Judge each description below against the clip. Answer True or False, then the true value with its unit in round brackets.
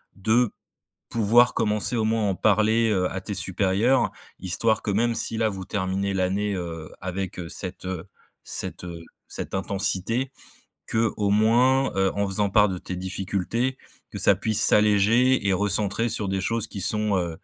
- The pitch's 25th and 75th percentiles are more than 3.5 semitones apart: False (2.9 semitones)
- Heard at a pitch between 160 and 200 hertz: False (100 Hz)